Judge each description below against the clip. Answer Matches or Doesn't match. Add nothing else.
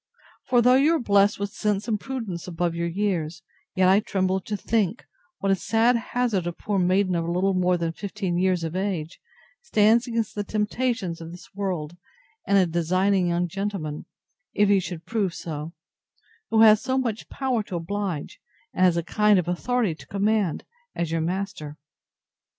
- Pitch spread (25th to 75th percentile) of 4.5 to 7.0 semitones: Doesn't match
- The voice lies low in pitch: Doesn't match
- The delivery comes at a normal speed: Matches